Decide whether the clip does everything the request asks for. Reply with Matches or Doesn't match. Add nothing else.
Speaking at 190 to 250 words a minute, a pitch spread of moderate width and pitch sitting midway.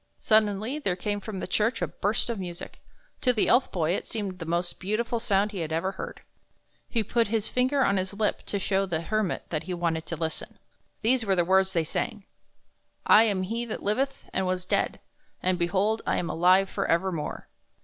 Doesn't match